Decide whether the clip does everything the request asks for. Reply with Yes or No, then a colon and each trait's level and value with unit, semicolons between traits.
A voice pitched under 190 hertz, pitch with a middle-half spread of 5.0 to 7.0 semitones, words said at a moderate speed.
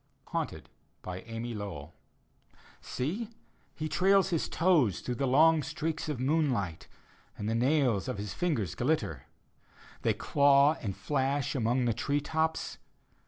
No: low, 135 Hz; wide, 5.6 semitones; slow, 130 wpm